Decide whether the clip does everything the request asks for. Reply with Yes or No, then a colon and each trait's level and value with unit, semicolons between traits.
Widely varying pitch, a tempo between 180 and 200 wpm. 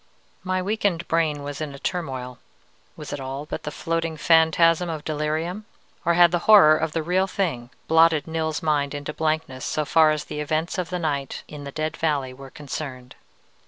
No: narrow, 2.5 semitones; average, 190 wpm